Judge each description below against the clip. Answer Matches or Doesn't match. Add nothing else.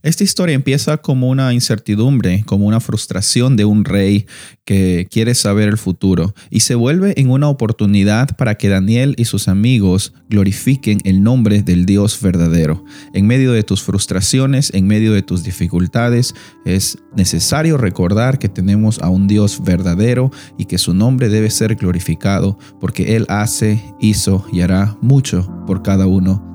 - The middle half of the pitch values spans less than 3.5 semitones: Doesn't match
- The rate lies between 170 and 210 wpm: Doesn't match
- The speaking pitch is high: Doesn't match